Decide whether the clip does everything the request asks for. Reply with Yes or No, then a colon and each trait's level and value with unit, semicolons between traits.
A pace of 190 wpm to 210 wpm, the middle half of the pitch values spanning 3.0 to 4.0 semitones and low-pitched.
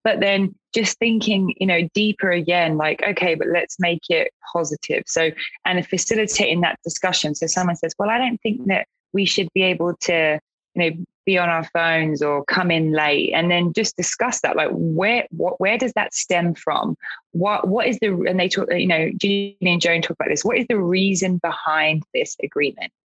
No: average, 200 wpm; average, 3.4 semitones; medium, 180 Hz